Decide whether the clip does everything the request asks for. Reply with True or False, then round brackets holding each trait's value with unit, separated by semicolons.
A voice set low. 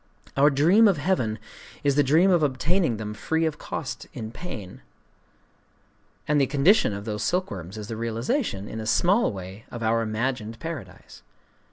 True (130 Hz)